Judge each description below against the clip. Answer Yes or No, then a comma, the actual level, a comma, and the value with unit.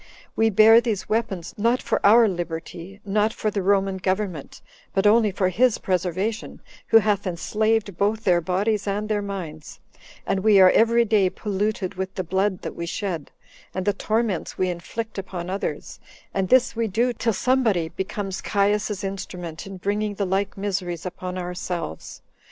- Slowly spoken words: No, average, 165 wpm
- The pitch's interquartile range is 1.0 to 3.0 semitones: Yes, average, 2.7 semitones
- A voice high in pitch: Yes, high, 195 Hz